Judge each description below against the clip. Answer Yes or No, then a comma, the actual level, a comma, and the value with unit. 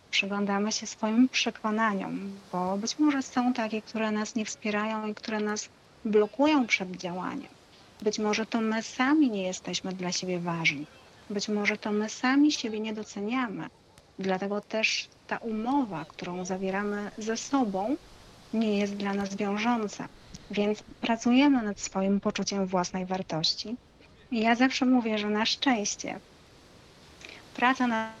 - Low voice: No, high, 215 Hz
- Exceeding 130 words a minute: Yes, average, 140 wpm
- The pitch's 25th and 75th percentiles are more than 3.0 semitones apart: No, average, 2.7 semitones